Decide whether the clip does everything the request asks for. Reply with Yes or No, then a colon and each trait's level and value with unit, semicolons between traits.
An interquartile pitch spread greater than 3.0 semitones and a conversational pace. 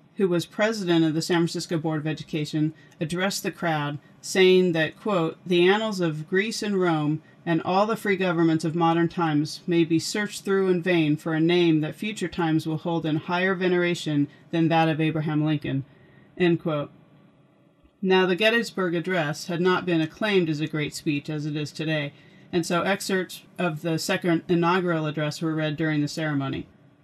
No: narrow, 2.6 semitones; average, 185 wpm